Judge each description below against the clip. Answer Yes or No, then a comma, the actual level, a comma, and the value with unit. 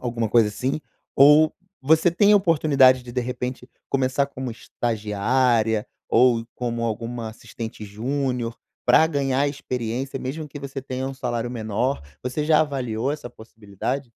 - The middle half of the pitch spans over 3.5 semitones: No, average, 3.1 semitones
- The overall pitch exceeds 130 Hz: No, low, 125 Hz